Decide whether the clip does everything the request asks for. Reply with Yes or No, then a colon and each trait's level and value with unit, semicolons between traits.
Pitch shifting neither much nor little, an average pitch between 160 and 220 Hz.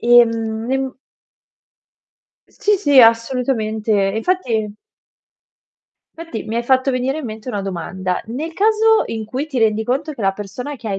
No: average, 3.9 semitones; high, 235 Hz